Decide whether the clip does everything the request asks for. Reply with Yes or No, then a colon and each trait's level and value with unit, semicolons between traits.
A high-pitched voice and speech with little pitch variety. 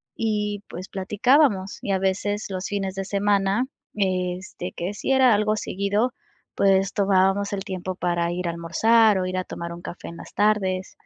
Yes: high, 195 Hz; narrow, 2.0 semitones